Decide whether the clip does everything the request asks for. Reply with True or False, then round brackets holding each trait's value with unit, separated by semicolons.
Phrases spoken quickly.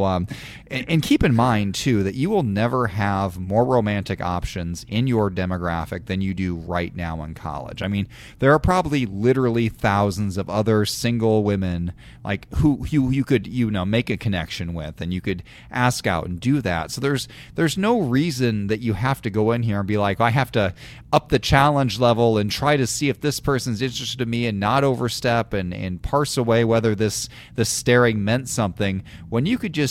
True (210 wpm)